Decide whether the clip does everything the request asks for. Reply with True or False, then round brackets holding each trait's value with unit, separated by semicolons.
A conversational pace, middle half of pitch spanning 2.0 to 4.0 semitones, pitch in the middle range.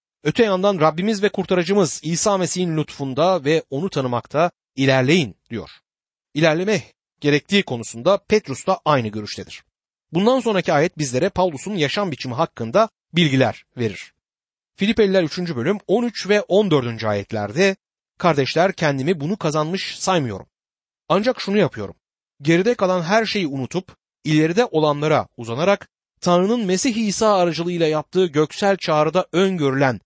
False (120 wpm; 5.4 semitones; 170 Hz)